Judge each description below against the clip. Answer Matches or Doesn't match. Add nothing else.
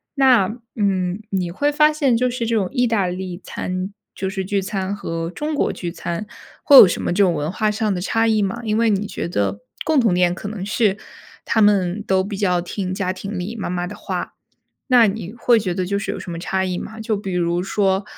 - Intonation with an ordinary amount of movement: Matches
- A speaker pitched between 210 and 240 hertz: Doesn't match